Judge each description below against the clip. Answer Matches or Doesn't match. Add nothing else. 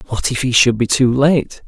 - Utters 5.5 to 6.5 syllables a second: Doesn't match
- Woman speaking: Doesn't match